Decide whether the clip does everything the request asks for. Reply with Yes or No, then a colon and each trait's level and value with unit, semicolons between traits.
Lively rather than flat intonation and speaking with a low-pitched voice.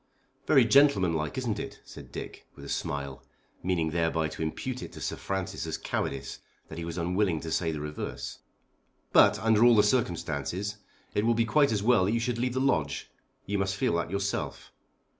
Yes: wide, 5.9 semitones; very low, 95 Hz